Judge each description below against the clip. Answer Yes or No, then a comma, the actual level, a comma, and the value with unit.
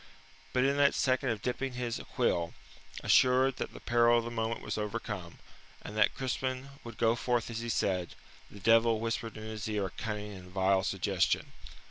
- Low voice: Yes, low, 115 Hz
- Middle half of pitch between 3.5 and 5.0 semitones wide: No, average, 3.1 semitones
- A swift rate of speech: No, average, 185 wpm